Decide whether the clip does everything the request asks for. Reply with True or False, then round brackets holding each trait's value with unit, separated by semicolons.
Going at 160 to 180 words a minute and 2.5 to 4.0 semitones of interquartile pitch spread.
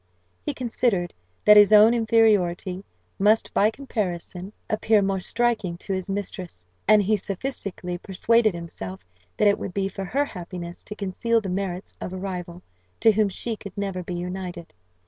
True (165 wpm; 3.2 semitones)